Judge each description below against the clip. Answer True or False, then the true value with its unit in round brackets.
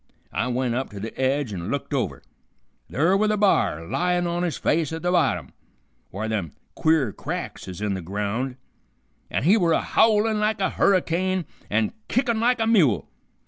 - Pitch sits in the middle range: True (160 Hz)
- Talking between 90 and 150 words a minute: False (185 wpm)